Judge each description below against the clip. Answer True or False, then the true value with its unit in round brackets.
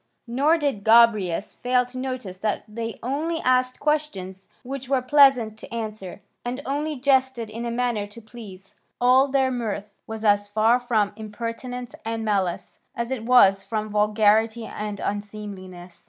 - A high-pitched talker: True (230 Hz)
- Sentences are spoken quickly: False (155 wpm)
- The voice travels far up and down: False (3.5 semitones)